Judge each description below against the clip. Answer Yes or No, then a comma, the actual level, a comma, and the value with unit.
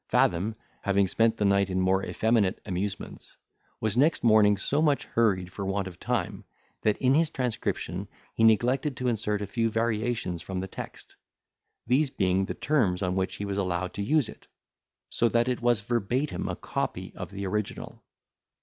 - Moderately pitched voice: No, low, 105 Hz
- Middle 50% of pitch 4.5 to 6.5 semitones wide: No, average, 3.8 semitones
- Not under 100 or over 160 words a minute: No, average, 175 wpm